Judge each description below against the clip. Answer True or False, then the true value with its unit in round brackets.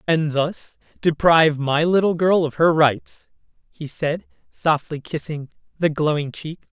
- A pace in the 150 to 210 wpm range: False (140 wpm)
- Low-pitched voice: False (155 Hz)